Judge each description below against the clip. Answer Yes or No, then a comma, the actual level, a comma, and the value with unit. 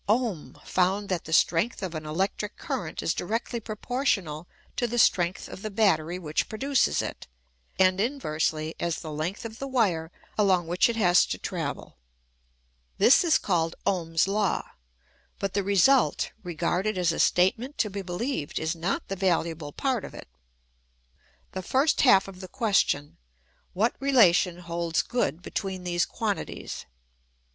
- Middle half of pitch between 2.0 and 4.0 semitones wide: No, average, 4.6 semitones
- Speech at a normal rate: Yes, average, 155 wpm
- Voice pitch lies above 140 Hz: Yes, medium, 185 Hz